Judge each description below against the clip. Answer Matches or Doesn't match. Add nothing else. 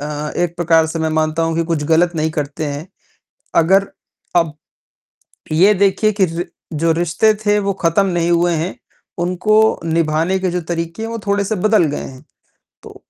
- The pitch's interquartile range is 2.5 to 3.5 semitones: Matches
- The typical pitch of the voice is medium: Matches